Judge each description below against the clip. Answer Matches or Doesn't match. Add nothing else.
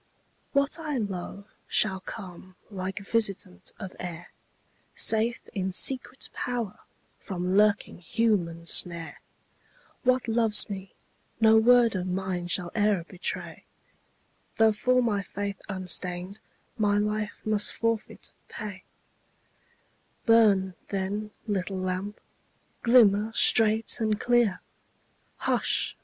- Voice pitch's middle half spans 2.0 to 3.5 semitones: Matches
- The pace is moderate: Doesn't match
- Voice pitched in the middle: Doesn't match